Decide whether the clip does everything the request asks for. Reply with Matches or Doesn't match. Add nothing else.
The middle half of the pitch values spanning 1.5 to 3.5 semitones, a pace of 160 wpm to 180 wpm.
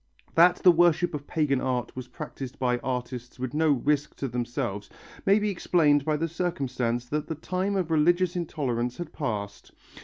Doesn't match